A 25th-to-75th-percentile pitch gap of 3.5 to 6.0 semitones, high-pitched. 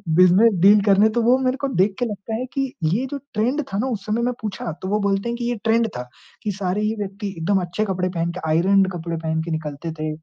Yes: average, 4.2 semitones; high, 200 Hz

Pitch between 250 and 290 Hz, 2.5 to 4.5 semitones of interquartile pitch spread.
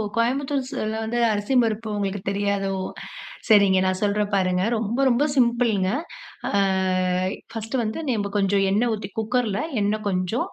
No: high, 215 Hz; average, 2.9 semitones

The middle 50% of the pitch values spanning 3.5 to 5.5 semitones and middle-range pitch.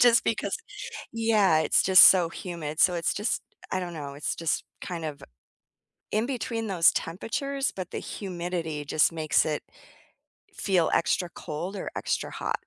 Yes: average, 4.4 semitones; medium, 180 Hz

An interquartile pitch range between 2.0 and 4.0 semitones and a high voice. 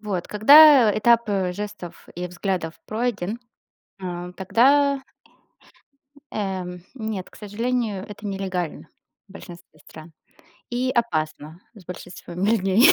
No: average, 4.4 semitones; high, 200 Hz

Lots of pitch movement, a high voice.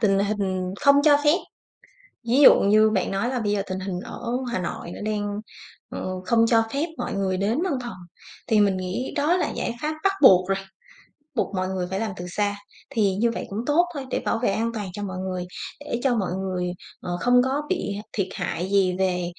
No: average, 4.1 semitones; high, 205 Hz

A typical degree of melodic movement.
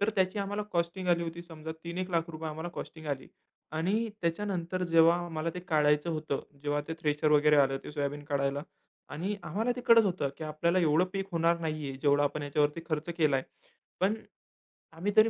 Yes: average, 3.4 semitones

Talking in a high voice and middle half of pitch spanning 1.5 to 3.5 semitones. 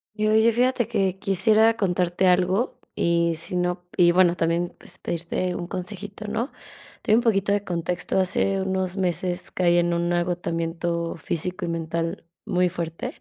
No: medium, 180 Hz; narrow, 2.4 semitones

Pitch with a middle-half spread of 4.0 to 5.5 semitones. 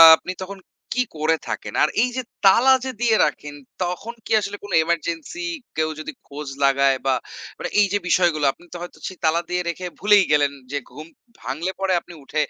Yes: average, 4.6 semitones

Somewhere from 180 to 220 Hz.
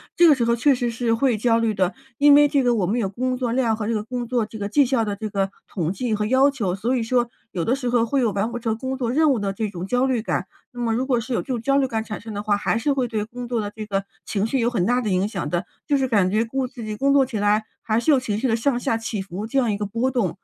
No: high, 230 Hz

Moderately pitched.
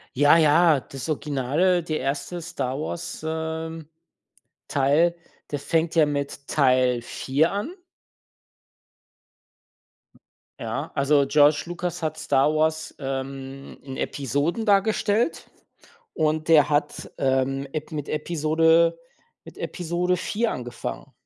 Yes: medium, 155 Hz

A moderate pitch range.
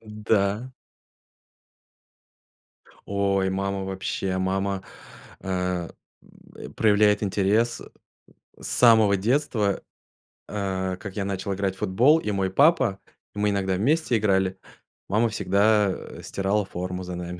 No: narrow, 2.0 semitones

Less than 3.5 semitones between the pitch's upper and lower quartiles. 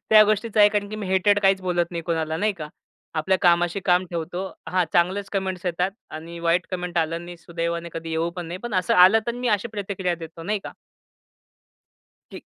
Yes: average, 2.8 semitones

